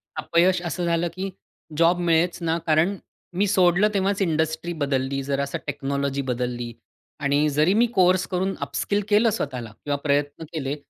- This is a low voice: No, medium, 160 Hz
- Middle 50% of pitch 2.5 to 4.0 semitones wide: No, average, 4.5 semitones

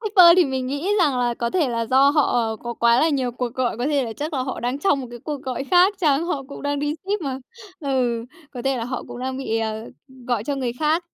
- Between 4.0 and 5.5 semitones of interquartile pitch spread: No, average, 3.5 semitones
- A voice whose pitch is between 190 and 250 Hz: No, very high, 265 Hz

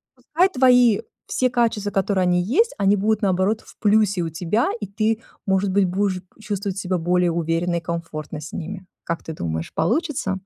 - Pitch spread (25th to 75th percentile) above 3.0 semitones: Yes, average, 3.6 semitones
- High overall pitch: Yes, high, 195 Hz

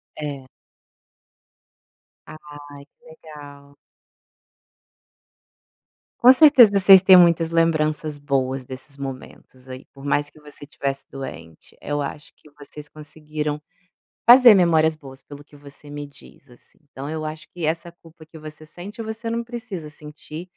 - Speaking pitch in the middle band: Yes, medium, 150 Hz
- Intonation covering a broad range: No, average, 3.0 semitones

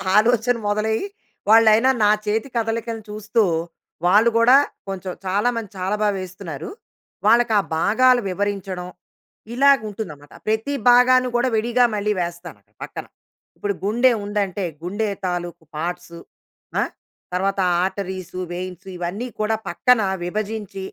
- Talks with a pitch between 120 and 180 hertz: No, high, 210 Hz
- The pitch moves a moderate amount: Yes, average, 3.7 semitones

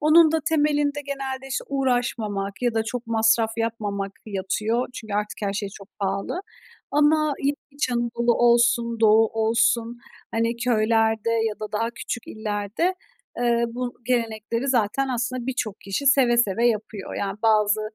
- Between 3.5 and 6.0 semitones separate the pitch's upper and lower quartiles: No, average, 2.7 semitones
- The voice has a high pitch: Yes, high, 230 Hz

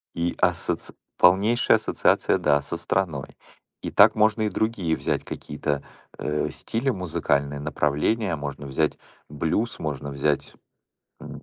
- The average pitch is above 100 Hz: No, very low, 80 Hz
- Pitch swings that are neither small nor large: No, wide, 6.2 semitones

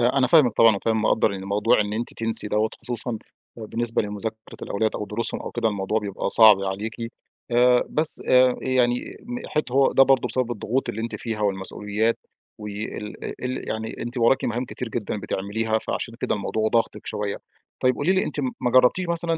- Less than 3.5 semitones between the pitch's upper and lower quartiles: Yes, average, 3.0 semitones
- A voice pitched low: Yes, low, 115 Hz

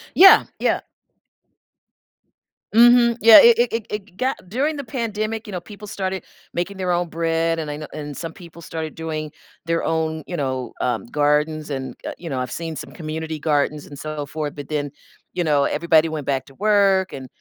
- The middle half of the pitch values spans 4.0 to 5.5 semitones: Yes, average, 5.1 semitones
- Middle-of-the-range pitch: Yes, medium, 165 Hz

